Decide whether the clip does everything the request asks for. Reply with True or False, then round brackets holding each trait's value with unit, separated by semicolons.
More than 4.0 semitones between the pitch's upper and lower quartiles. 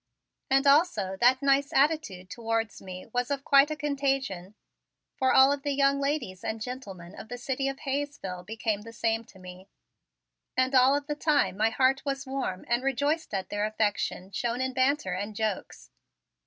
True (5.1 semitones)